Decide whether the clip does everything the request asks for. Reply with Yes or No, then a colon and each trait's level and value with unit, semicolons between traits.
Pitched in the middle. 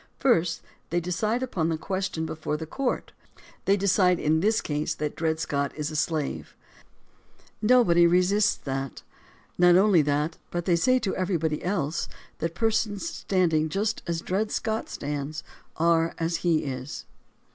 Yes: medium, 170 Hz